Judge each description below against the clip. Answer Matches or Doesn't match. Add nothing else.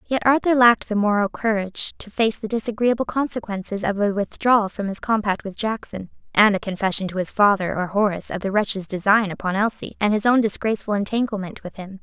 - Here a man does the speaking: Doesn't match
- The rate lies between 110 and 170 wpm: Doesn't match